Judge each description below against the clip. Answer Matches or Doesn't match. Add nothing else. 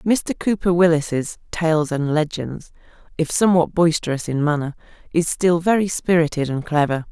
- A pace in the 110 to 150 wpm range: Matches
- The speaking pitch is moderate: Matches